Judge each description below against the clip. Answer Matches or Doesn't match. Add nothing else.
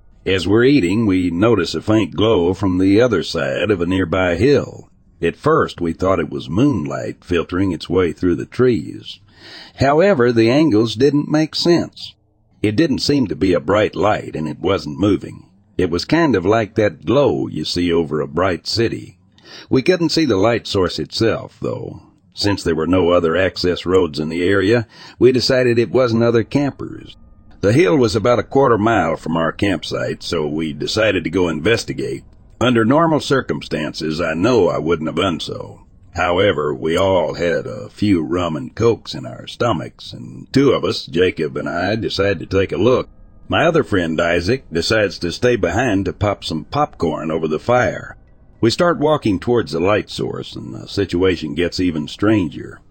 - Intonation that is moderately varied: Doesn't match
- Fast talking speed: Doesn't match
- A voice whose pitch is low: Matches